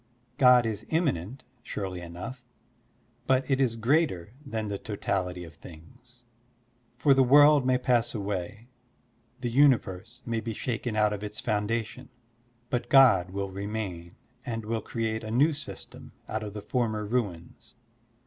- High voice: No, low, 110 Hz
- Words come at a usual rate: Yes, average, 145 wpm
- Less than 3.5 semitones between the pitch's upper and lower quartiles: No, average, 3.9 semitones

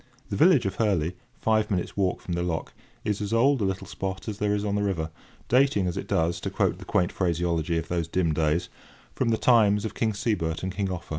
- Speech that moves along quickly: Yes, fast, 235 wpm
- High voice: No, very low, 95 Hz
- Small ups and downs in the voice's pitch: No, average, 3.6 semitones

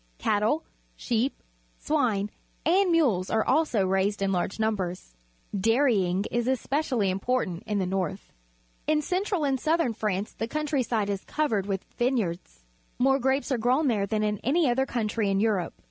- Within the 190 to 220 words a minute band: No, average, 150 wpm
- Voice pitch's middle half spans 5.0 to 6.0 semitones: Yes, wide, 5.4 semitones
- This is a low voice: No, high, 225 Hz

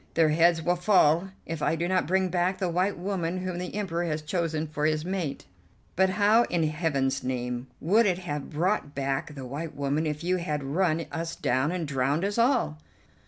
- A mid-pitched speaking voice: Yes, medium, 165 Hz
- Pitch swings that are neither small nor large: Yes, average, 3.6 semitones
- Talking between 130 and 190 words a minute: No, average, 200 wpm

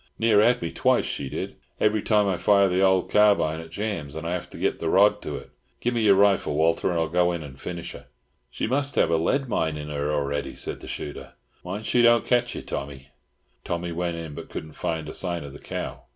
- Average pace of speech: No, fast, 240 wpm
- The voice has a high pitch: No, very low, 85 Hz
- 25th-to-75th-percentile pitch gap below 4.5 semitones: No, average, 5.0 semitones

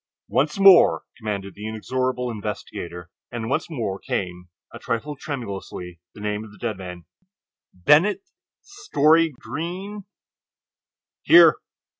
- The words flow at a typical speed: No, slow, 105 wpm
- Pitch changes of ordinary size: No, wide, 7.8 semitones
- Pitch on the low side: Yes, low, 115 Hz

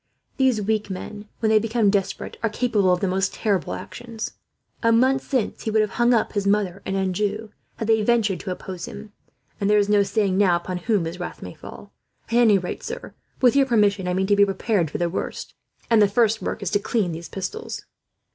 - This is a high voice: Yes, high, 205 Hz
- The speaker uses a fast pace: Yes, fast, 220 wpm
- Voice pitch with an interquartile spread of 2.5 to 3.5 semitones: Yes, average, 2.8 semitones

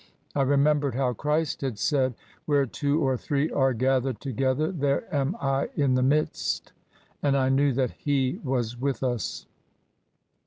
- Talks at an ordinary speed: Yes, average, 165 wpm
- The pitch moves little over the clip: Yes, narrow, 1.8 semitones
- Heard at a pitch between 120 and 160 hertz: Yes, low, 135 Hz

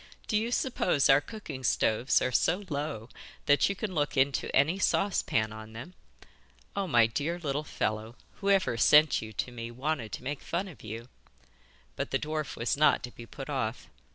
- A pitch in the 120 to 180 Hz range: Yes, medium, 140 Hz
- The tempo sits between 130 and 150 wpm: No, average, 180 wpm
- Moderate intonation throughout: No, wide, 5.8 semitones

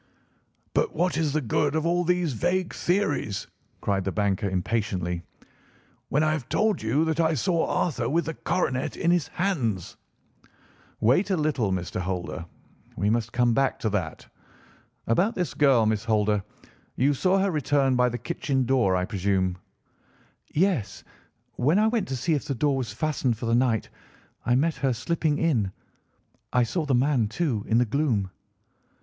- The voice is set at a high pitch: No, low, 130 Hz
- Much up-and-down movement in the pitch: Yes, wide, 6.8 semitones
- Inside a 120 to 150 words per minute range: No, average, 170 wpm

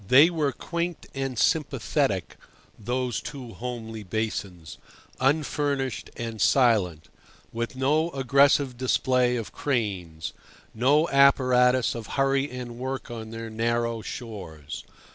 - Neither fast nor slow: No, slow, 110 wpm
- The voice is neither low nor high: No, low, 125 Hz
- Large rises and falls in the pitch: No, average, 3.6 semitones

